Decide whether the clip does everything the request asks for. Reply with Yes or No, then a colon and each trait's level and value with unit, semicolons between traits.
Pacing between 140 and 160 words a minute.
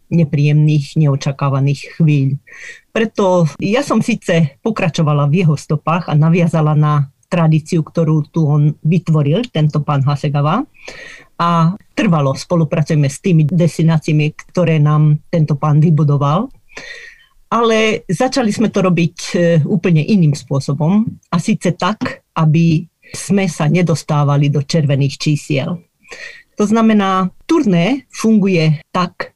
No: average, 115 wpm